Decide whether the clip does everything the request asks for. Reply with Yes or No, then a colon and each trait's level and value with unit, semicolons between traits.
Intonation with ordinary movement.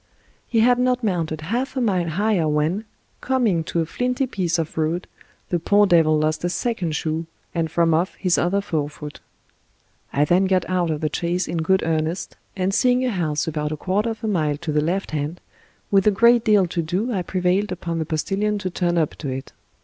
Yes: average, 4.4 semitones